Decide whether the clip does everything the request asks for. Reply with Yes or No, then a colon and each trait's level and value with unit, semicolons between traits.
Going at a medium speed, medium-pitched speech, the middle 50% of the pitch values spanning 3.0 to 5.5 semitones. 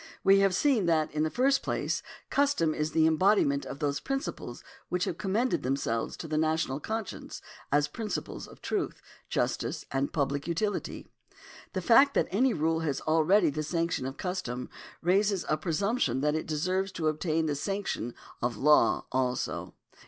Yes: average, 165 wpm; medium, 160 Hz; average, 5.0 semitones